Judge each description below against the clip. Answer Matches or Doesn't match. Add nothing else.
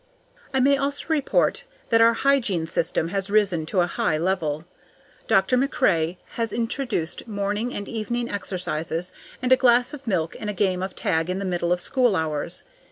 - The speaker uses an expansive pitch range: Matches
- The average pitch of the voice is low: Doesn't match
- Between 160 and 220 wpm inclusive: Matches